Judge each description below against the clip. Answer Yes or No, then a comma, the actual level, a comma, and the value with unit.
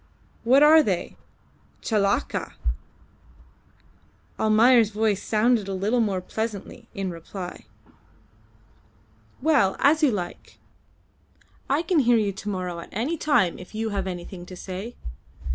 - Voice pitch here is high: Yes, high, 215 Hz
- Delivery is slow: Yes, slow, 125 wpm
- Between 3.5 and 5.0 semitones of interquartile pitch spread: Yes, average, 4.4 semitones